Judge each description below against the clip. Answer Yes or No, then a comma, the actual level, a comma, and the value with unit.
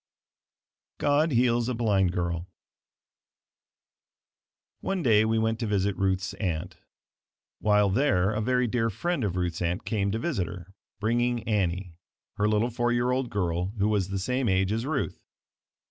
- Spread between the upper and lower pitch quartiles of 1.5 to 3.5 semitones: No, average, 4.2 semitones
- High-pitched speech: No, low, 105 Hz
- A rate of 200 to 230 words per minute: No, average, 155 wpm